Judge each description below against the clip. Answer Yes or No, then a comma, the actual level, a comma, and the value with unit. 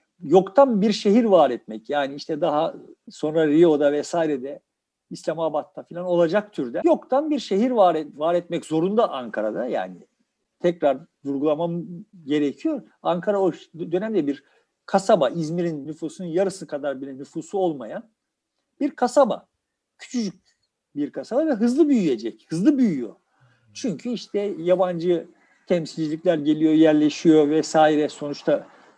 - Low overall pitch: No, medium, 175 Hz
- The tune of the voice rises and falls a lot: Yes, wide, 6.1 semitones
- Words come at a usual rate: Yes, average, 120 wpm